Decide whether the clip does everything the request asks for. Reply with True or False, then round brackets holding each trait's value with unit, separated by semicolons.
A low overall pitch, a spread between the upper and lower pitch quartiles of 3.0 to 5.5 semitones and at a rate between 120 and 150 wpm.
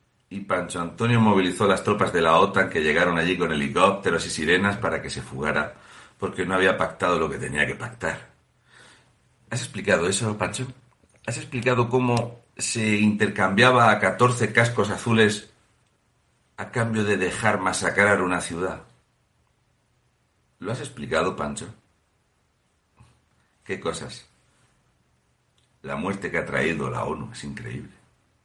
True (105 Hz; 3.9 semitones; 135 wpm)